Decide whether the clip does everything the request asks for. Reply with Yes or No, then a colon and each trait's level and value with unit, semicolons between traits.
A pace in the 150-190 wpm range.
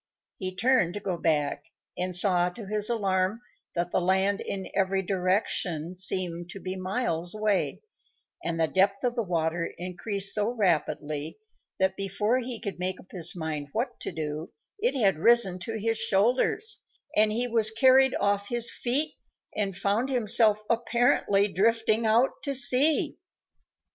Yes: average, 155 wpm